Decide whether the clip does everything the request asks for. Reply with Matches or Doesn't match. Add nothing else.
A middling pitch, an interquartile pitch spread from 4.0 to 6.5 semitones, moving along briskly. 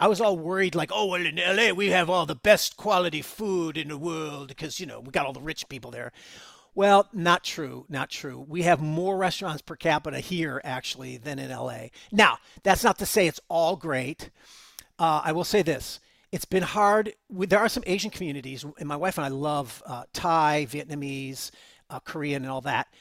Matches